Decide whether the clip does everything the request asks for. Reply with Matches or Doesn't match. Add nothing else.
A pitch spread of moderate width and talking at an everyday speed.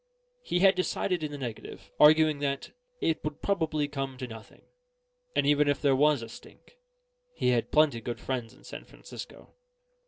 Matches